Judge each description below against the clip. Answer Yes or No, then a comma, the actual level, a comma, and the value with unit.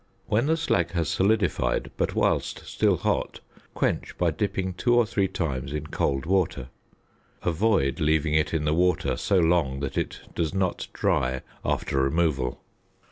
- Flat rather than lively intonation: No, average, 4.9 semitones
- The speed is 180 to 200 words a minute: No, average, 155 wpm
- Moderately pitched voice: No, very low, 85 Hz